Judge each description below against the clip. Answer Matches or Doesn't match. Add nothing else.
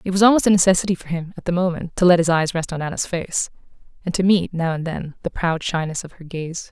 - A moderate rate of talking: Doesn't match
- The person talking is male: Doesn't match